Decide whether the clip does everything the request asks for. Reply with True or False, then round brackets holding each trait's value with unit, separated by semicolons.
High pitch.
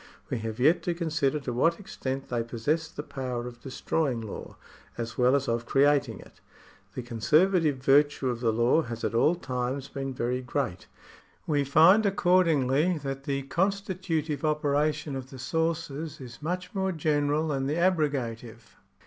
False (140 Hz)